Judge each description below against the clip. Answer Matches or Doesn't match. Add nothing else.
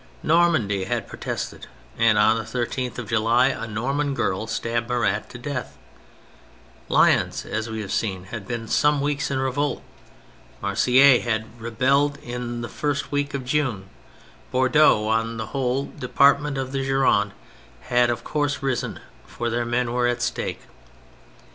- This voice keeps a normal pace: Matches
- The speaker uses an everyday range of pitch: Matches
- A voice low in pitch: Matches